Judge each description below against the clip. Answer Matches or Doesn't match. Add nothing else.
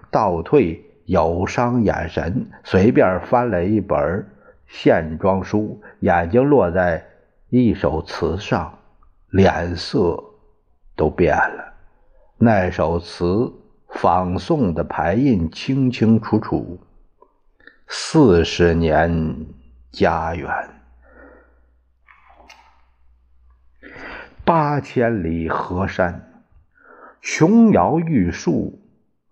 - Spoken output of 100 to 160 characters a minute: Matches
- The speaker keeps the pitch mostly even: Doesn't match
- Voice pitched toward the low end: Matches